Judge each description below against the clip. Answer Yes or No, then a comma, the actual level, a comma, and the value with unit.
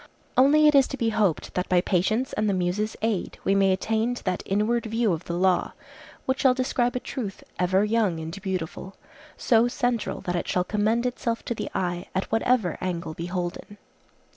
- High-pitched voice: Yes, high, 210 Hz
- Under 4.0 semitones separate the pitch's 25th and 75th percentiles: No, average, 4.6 semitones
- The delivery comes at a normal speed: Yes, average, 190 wpm